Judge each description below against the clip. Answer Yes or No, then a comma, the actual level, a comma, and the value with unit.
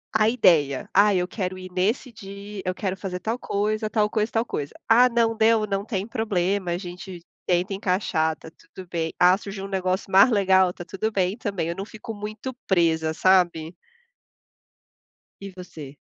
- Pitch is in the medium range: No, high, 195 Hz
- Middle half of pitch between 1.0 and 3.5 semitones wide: Yes, average, 2.9 semitones